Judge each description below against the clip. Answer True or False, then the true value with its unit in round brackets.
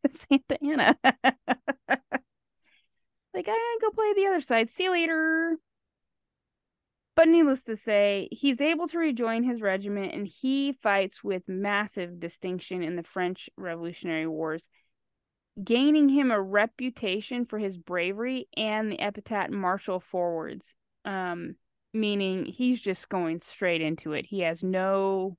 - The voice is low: False (210 Hz)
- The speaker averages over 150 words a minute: False (135 wpm)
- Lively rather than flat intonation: True (6.4 semitones)